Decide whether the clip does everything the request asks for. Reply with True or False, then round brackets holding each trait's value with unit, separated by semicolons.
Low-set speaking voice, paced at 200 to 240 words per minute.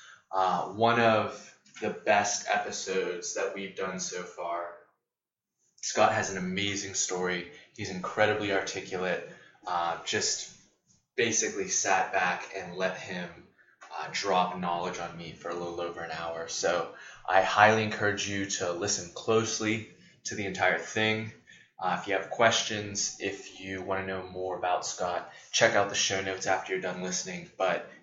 False (95 Hz; 155 wpm)